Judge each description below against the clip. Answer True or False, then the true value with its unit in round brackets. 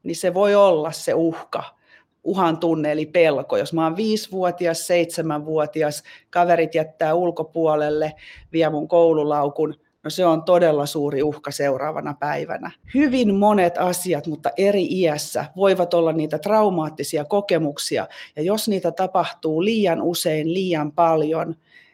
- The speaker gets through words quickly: False (130 wpm)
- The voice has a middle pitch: True (165 Hz)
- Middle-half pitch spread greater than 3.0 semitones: False (2.7 semitones)